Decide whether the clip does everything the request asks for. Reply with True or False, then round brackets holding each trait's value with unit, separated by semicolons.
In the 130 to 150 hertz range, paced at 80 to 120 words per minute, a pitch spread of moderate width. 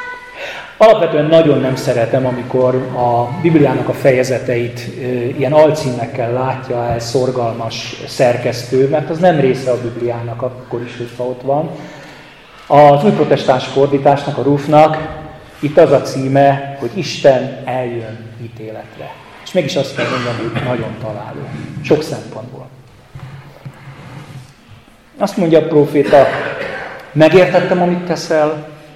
True (135 Hz; 115 wpm; 3.6 semitones)